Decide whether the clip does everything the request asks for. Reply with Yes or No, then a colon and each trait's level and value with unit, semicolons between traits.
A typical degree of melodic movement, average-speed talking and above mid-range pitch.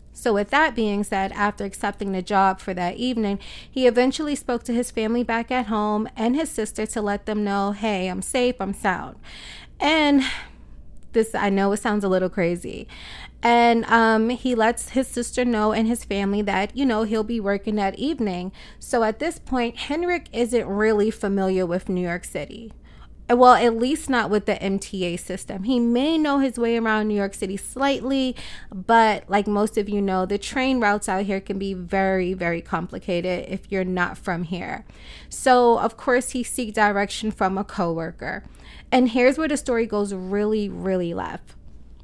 Yes: average, 3.8 semitones; average, 185 wpm; high, 215 Hz